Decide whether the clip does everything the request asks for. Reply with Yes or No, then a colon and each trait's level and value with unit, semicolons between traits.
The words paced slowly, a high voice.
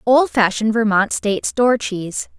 Yes: slow, 125 wpm; high, 220 Hz